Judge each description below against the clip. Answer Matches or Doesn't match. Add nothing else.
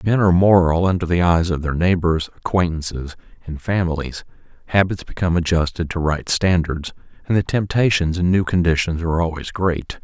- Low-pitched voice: Matches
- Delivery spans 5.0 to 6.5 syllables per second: Matches